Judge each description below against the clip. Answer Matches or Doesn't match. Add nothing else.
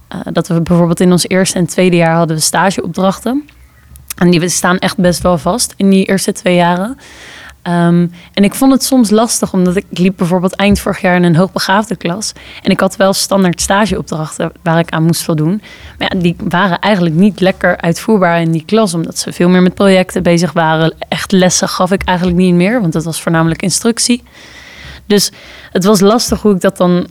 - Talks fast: Matches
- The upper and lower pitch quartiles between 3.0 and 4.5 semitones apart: Doesn't match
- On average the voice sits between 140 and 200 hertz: Matches